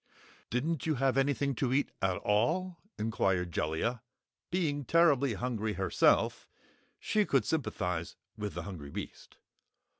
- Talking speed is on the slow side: Yes, slow, 125 wpm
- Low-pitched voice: Yes, low, 125 Hz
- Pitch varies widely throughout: Yes, wide, 6.4 semitones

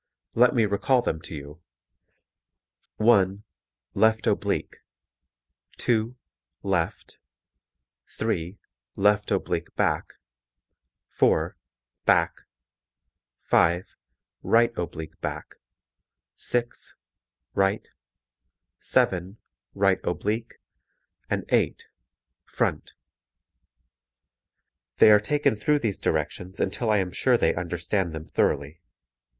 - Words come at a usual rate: No, slow, 90 wpm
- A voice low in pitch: Yes, low, 100 Hz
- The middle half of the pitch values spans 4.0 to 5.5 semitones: Yes, average, 4.3 semitones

